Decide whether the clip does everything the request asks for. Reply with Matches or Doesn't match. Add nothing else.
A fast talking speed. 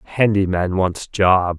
Doesn't match